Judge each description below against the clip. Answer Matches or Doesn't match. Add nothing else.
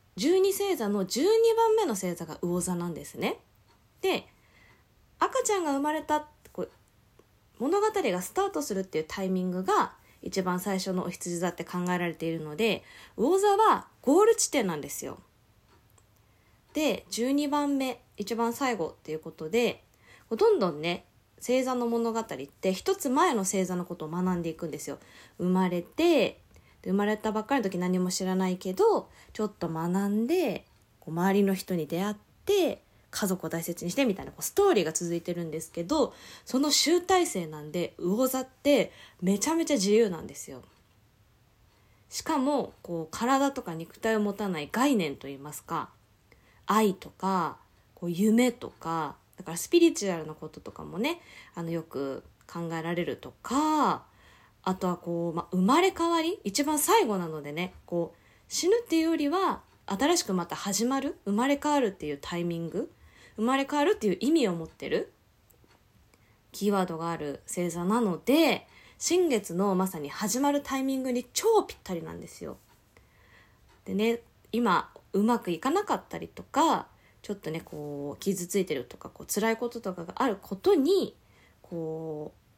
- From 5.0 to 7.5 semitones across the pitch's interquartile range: Doesn't match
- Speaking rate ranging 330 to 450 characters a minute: Doesn't match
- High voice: Matches